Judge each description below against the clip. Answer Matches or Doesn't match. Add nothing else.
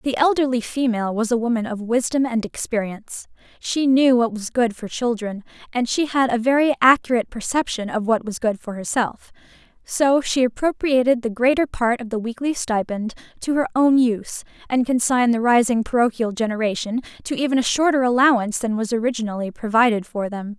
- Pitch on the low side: Doesn't match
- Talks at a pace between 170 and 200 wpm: Matches